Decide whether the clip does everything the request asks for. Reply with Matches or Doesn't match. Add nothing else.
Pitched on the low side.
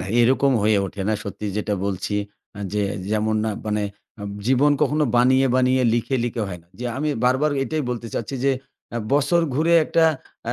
Matches